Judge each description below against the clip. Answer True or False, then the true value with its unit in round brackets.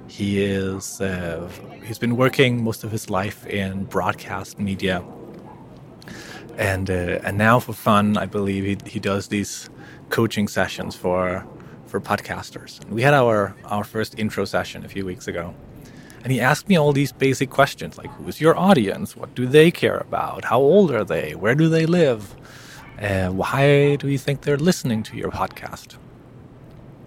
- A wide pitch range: True (5.9 semitones)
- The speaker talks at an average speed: True (170 wpm)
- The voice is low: True (110 Hz)